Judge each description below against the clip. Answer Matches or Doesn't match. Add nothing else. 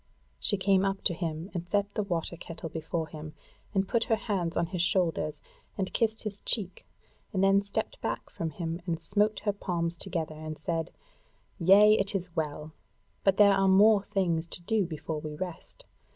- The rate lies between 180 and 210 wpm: Matches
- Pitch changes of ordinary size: Matches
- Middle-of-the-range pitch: Matches